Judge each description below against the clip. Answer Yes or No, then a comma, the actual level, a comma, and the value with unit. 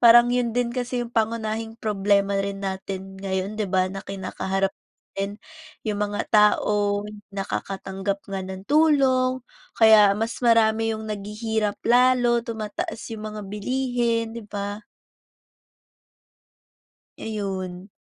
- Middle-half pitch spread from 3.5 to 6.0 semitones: No, average, 2.9 semitones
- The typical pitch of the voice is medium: No, high, 215 Hz